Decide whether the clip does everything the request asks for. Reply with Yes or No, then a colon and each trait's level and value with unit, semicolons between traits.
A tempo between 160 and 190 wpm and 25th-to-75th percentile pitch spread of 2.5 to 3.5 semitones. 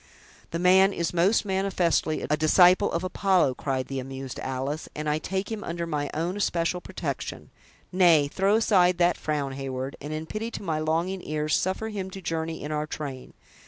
No: average, 185 wpm; average, 3.9 semitones